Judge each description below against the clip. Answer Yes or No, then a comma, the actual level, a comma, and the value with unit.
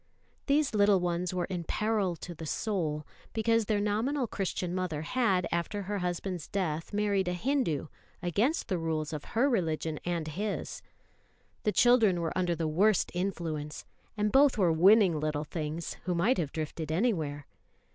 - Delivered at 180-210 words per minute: No, average, 160 wpm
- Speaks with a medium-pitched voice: Yes, medium, 180 Hz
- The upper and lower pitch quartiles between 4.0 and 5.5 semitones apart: Yes, average, 4.5 semitones